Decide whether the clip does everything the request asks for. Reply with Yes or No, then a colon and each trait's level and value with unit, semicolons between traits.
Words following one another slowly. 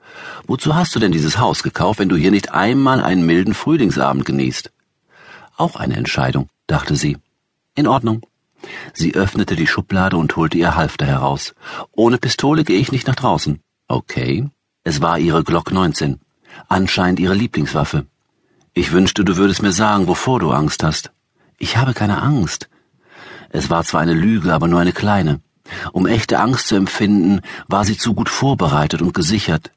No: average, 165 wpm